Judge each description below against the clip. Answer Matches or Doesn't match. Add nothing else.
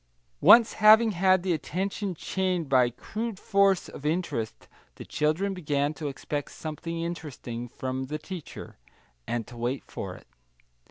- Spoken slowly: Doesn't match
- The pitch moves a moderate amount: Doesn't match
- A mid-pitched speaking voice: Matches